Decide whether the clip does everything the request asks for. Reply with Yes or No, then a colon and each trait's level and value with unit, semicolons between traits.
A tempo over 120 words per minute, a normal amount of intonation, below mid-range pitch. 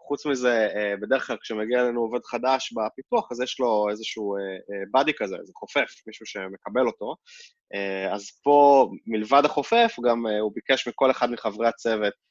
Yes: fast, 150 wpm; average, 4.0 semitones; low, 120 Hz